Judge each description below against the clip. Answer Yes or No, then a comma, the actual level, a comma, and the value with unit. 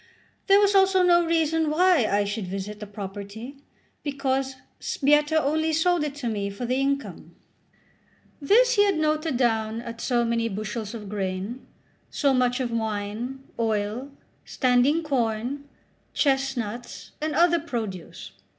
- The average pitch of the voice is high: Yes, very high, 255 Hz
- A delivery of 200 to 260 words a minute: No, average, 140 wpm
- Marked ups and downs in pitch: Yes, wide, 5.9 semitones